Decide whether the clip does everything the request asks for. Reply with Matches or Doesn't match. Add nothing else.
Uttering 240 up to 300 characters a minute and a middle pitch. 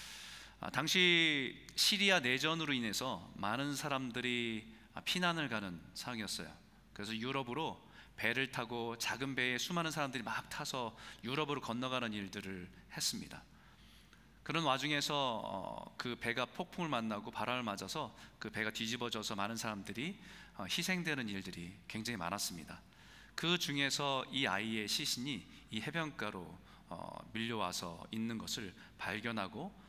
Doesn't match